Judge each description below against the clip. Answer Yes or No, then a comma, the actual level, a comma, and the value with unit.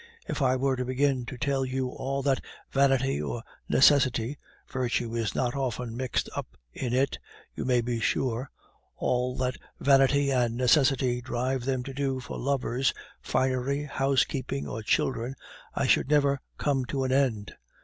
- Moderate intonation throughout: No, narrow, 1.7 semitones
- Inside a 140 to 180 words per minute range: Yes, average, 160 wpm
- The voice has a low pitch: Yes, low, 130 Hz